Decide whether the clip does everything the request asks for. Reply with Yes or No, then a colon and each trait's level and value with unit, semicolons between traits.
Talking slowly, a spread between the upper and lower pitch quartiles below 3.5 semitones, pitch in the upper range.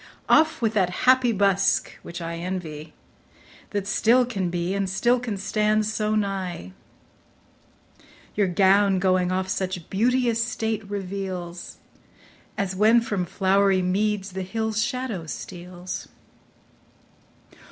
Yes: slow, 120 wpm; average, 2.9 semitones; high, 195 Hz